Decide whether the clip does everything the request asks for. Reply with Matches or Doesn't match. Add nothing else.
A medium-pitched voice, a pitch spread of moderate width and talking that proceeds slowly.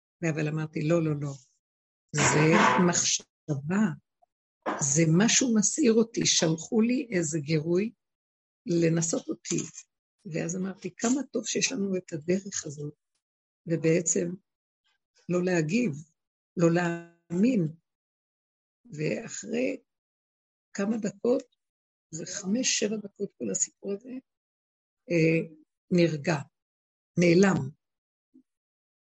Matches